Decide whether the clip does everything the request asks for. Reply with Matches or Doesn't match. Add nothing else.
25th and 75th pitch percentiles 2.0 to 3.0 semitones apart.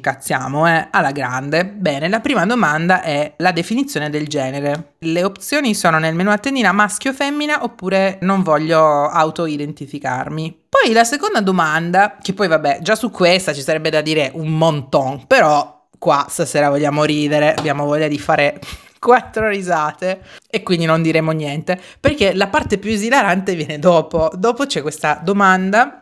Doesn't match